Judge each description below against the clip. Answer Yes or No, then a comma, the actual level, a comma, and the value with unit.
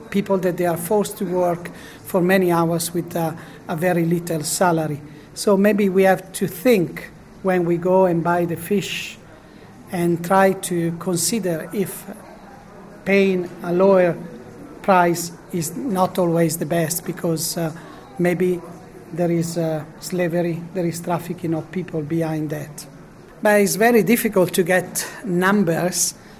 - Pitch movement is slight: Yes, narrow, 2.2 semitones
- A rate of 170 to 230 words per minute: No, average, 145 wpm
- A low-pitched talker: No, medium, 175 Hz